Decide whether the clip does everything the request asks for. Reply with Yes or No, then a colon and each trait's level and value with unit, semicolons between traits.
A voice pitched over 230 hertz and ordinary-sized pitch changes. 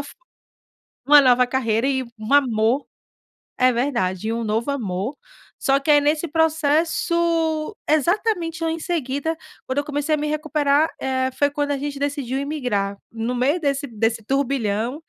Yes: very high, 280 Hz; average, 3.8 semitones